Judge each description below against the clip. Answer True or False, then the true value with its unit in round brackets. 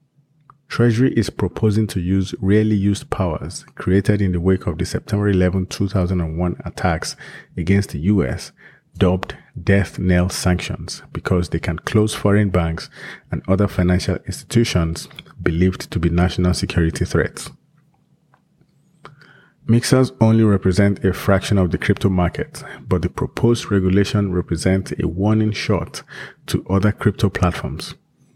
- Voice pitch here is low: True (100 Hz)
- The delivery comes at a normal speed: False (130 wpm)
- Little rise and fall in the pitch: False (3.3 semitones)